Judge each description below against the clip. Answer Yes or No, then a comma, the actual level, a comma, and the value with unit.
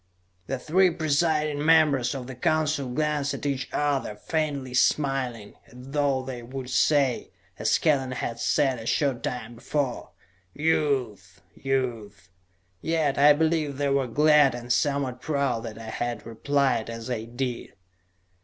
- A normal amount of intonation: Yes, average, 3.4 semitones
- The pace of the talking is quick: No, average, 145 wpm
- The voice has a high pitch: No, low, 135 Hz